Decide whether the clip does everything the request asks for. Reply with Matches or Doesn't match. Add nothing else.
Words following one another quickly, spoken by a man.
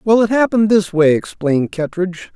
Doesn't match